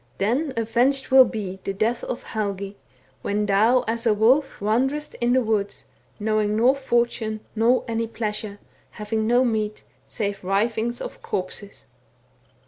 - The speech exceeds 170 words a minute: No, average, 145 wpm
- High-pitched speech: Yes, high, 220 Hz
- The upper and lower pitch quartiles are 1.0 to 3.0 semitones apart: Yes, narrow, 2.5 semitones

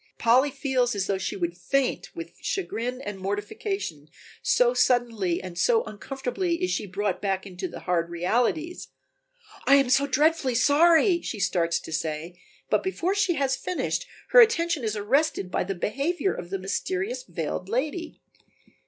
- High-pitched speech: Yes, very high, 250 Hz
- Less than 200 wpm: Yes, average, 160 wpm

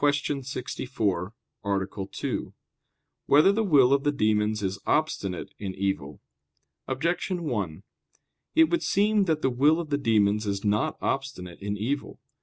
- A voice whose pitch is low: Yes, low, 125 Hz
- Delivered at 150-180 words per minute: No, average, 140 wpm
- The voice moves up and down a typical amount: No, wide, 6.5 semitones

